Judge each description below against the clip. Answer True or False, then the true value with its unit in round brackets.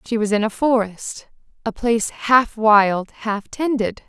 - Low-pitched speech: False (225 Hz)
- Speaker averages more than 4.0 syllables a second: False (3.9 syllables/s)